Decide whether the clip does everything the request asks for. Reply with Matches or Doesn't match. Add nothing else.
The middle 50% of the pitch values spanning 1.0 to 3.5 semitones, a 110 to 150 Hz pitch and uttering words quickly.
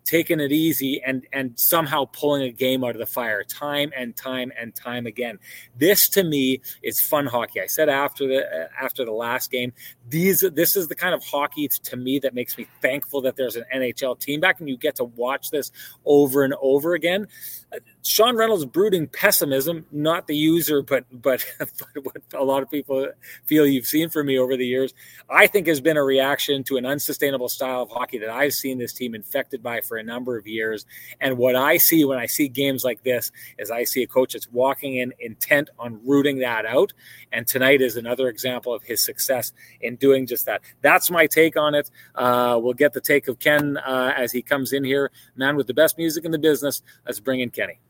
Matches